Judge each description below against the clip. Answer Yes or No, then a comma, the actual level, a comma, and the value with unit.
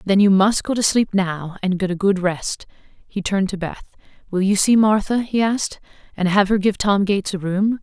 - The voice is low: No, high, 195 Hz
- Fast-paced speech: Yes, fast, 230 wpm